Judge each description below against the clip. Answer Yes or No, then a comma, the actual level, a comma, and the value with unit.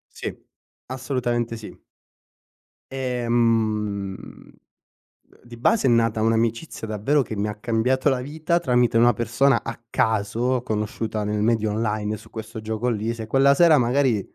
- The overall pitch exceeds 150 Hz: No, low, 115 Hz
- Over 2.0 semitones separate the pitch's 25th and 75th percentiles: Yes, narrow, 2.6 semitones